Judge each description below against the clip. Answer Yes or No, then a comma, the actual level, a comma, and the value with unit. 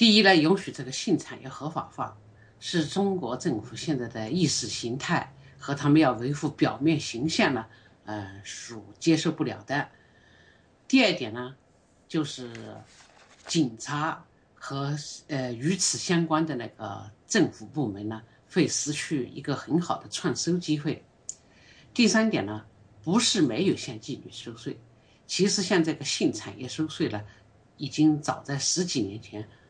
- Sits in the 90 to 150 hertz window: Yes, low, 135 Hz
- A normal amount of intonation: No, wide, 6.2 semitones